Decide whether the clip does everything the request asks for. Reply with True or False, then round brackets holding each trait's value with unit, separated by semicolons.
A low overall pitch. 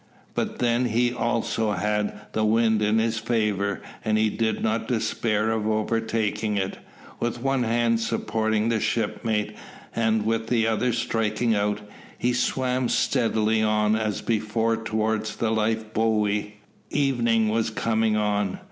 True (110 Hz)